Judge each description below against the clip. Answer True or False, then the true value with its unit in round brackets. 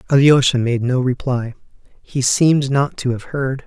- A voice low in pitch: True (130 Hz)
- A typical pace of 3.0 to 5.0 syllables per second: True (4.6 syllables/s)